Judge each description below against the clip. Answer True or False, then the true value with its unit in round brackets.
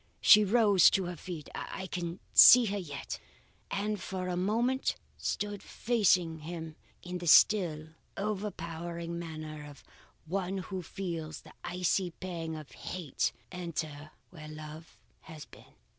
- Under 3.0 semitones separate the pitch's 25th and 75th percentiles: False (3.5 semitones)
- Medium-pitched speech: True (175 Hz)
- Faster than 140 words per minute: False (135 wpm)